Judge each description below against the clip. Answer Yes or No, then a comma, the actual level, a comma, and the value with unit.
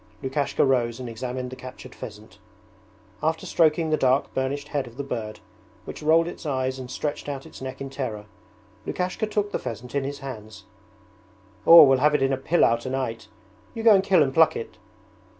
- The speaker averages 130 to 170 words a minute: No, average, 185 wpm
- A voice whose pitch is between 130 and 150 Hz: Yes, low, 135 Hz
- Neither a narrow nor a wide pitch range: Yes, average, 3.4 semitones